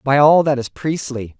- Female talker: No, male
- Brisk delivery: Yes, fast, 215 wpm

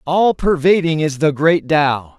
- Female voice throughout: No, male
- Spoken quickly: No, average, 165 wpm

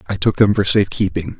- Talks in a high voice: No, very low, 95 Hz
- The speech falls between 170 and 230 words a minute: No, fast, 260 wpm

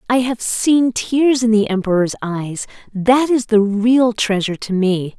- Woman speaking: Yes, female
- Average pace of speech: Yes, average, 160 wpm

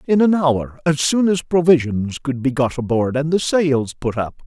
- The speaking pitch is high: No, medium, 145 Hz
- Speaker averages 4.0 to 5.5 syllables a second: Yes, 4.7 syllables/s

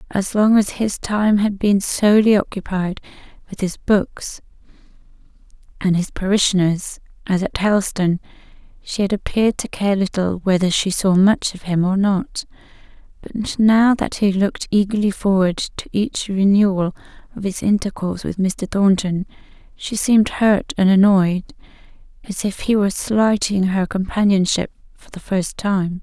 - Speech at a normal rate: Yes, average, 150 wpm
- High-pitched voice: Yes, high, 195 Hz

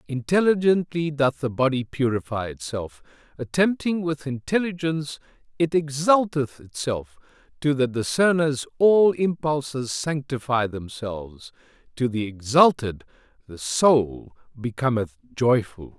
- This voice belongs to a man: Yes, male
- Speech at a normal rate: No, slow, 100 wpm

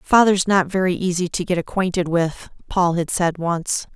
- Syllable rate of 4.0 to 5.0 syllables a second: Yes, 4.6 syllables/s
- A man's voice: No, female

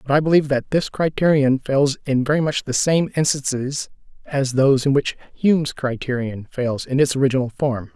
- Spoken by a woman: No, male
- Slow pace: No, average, 180 wpm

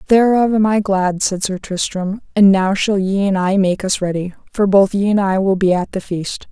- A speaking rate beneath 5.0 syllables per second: Yes, 4.8 syllables/s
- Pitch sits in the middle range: No, high, 195 Hz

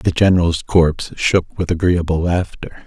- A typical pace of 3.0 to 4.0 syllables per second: No, 4.7 syllables/s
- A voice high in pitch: No, very low, 85 Hz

